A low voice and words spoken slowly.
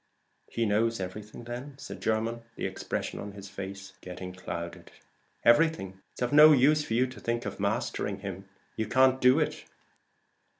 No: low, 115 Hz; average, 165 wpm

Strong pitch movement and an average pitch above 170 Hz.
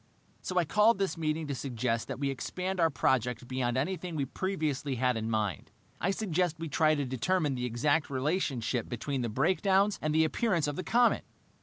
No: wide, 6.0 semitones; medium, 150 Hz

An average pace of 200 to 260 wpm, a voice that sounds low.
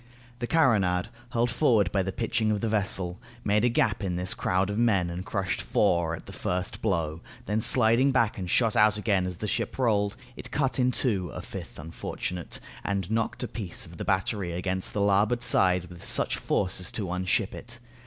Yes: fast, 205 wpm; low, 100 Hz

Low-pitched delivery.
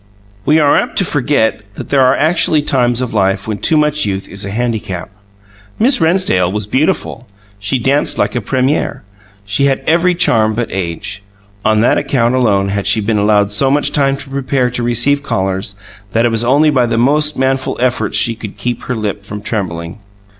Yes: low, 120 Hz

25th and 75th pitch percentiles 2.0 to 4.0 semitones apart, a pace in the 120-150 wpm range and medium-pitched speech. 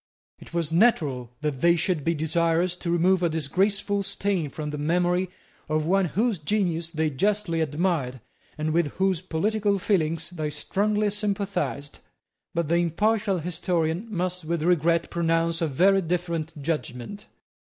Yes: average, 3.4 semitones; average, 145 wpm; medium, 170 Hz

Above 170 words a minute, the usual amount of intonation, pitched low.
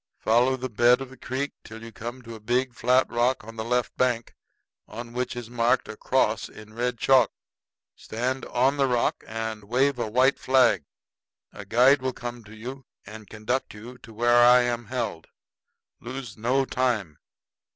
No: average, 180 wpm; narrow, 2.3 semitones; low, 120 Hz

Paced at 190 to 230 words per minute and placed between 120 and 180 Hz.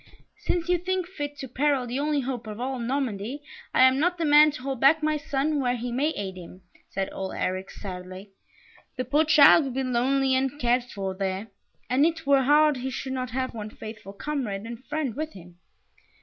No: fast, 205 wpm; very high, 260 Hz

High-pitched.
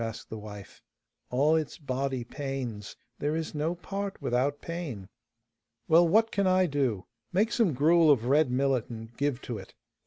No: medium, 140 Hz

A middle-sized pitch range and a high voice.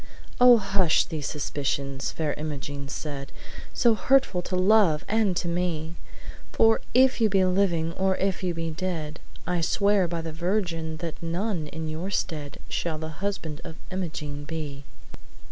No: average, 3.7 semitones; medium, 170 Hz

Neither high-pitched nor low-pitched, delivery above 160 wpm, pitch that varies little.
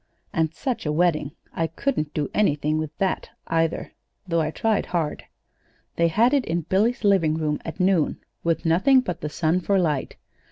No: medium, 165 Hz; average, 175 wpm; average, 3.8 semitones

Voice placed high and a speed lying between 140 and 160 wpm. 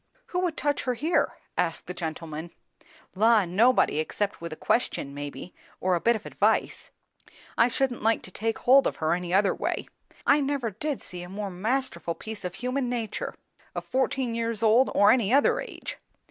No: high, 220 Hz; average, 185 wpm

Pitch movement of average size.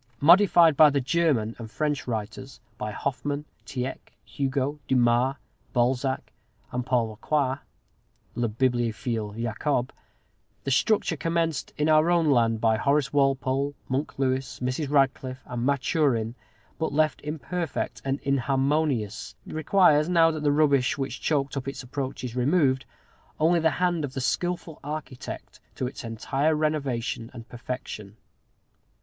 Yes: average, 3.5 semitones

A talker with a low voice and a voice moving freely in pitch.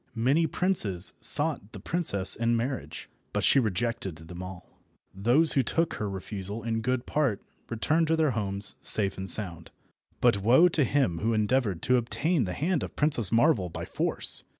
Yes: low, 115 Hz; wide, 6.7 semitones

